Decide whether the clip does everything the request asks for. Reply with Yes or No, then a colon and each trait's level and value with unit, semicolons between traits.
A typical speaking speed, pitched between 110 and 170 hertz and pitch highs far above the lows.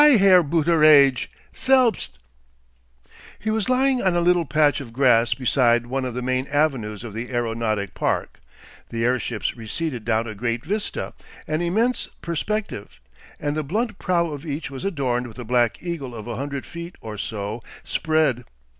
Yes: average, 165 wpm; medium, 140 Hz; wide, 6.4 semitones